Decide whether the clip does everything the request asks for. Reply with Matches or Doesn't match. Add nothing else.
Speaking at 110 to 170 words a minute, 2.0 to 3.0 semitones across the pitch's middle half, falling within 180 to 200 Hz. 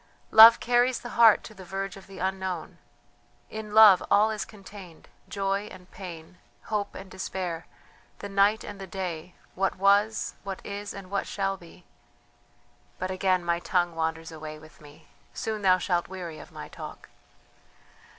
Matches